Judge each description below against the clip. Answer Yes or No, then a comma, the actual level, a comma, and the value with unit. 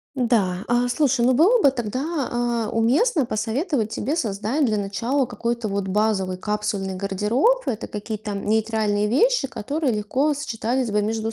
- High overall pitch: Yes, high, 230 Hz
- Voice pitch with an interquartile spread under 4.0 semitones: No, average, 4.3 semitones